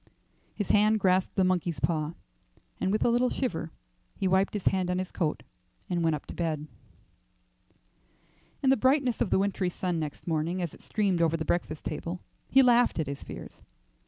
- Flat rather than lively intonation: No, average, 4.1 semitones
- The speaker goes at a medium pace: Yes, average, 190 wpm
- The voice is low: No, medium, 180 Hz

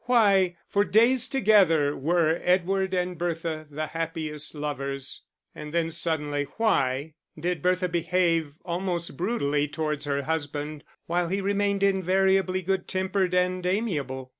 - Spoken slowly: Yes, slow, 130 wpm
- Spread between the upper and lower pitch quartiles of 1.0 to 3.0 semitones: No, average, 4.0 semitones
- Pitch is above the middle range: No, medium, 170 Hz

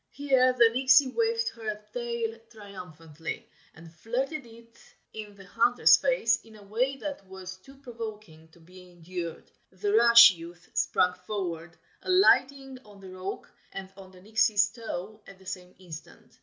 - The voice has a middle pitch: No, high, 210 Hz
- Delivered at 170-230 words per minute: No, average, 155 wpm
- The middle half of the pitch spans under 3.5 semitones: No, average, 4.8 semitones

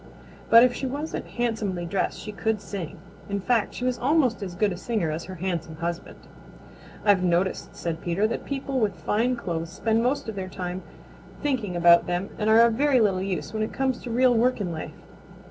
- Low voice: No, high, 210 Hz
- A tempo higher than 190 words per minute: Yes, fast, 205 wpm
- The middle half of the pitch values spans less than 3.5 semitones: No, average, 5.2 semitones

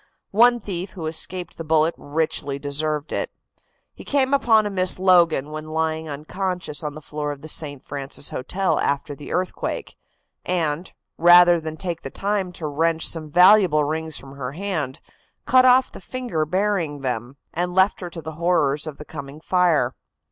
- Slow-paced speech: No, average, 175 wpm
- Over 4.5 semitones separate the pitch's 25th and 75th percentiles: No, average, 3.7 semitones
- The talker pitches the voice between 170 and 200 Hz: No, medium, 160 Hz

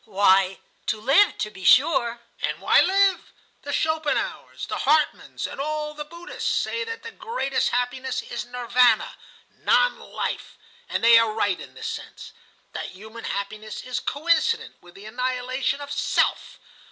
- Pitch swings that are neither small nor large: No, wide, 5.8 semitones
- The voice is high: Yes, very high, 255 Hz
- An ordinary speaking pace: Yes, average, 150 wpm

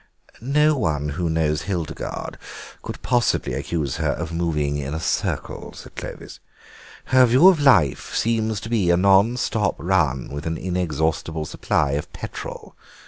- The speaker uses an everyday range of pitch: No, wide, 6.7 semitones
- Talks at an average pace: Yes, average, 150 wpm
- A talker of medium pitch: No, very low, 85 Hz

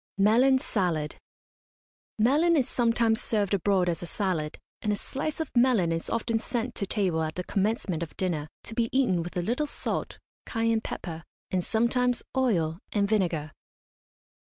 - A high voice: Yes, high, 210 Hz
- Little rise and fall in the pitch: No, average, 5.3 semitones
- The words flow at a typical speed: Yes, average, 160 wpm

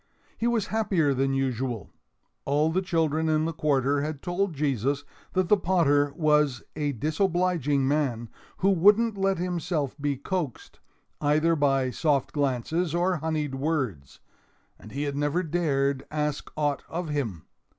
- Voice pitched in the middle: Yes, medium, 150 Hz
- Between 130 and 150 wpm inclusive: Yes, average, 145 wpm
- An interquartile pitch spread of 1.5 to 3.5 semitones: No, average, 3.9 semitones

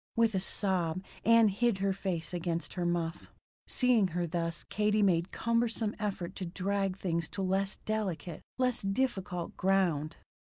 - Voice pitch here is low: No, high, 190 Hz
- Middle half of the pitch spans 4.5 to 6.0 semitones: No, average, 3.5 semitones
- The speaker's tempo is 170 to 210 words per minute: No, average, 145 wpm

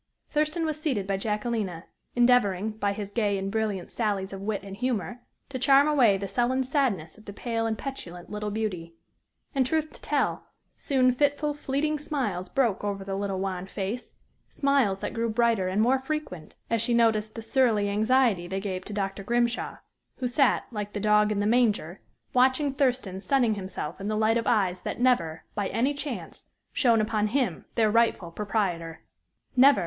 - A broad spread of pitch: No, average, 4.4 semitones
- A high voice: Yes, high, 220 Hz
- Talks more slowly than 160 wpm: No, average, 180 wpm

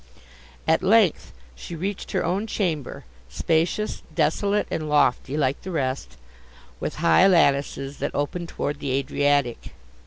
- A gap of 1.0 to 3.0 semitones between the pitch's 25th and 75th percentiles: No, average, 4.8 semitones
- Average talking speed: No, slow, 130 wpm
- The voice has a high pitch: No, medium, 155 Hz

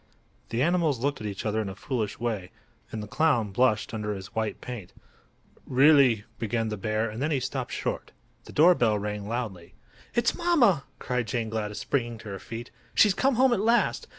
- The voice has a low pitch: Yes, low, 115 Hz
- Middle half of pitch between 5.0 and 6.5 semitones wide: Yes, average, 5.3 semitones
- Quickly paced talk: No, average, 195 wpm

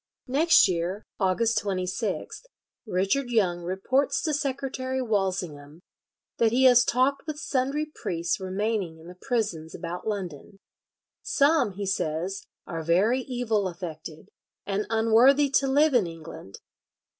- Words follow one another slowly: Yes, slow, 125 wpm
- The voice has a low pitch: No, high, 210 Hz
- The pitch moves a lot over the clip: Yes, wide, 6.4 semitones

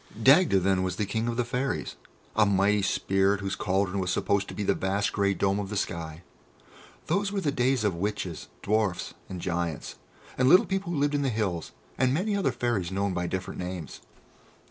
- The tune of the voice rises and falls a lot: No, average, 5.0 semitones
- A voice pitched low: Yes, low, 100 Hz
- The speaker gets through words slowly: No, average, 200 wpm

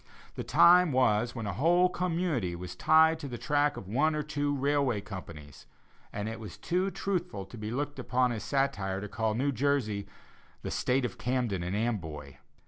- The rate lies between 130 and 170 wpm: No, average, 185 wpm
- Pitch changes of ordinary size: No, wide, 6.1 semitones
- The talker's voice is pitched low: Yes, low, 125 Hz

